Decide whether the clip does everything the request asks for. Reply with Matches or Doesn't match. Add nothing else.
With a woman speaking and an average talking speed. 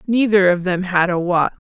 Doesn't match